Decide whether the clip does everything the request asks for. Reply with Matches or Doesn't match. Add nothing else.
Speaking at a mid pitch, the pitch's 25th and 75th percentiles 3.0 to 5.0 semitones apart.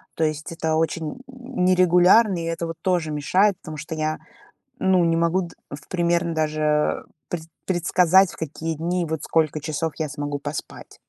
Doesn't match